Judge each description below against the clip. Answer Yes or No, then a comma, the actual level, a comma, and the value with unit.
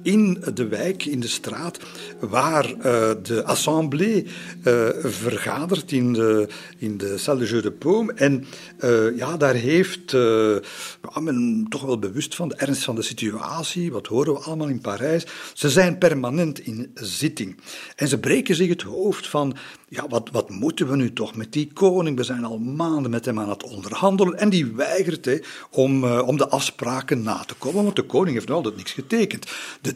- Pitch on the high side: No, medium, 140 Hz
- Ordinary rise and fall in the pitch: No, wide, 6.5 semitones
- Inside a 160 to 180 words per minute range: No, average, 190 wpm